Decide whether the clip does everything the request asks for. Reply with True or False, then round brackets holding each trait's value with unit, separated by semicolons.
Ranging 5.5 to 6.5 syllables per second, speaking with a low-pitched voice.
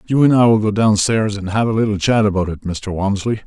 True (5.8 syllables/s; 105 Hz)